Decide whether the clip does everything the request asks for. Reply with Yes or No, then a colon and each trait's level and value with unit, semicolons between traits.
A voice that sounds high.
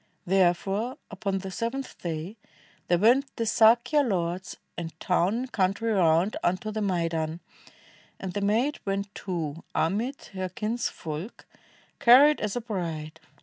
Yes: high, 195 Hz